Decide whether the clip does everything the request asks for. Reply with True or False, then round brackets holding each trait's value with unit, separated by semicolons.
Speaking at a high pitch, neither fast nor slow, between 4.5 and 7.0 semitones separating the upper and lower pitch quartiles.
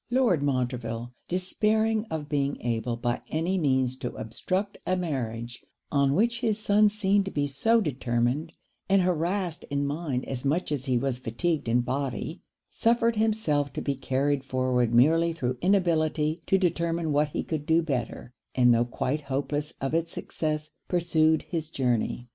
False (150 Hz; 160 wpm; 5.5 semitones)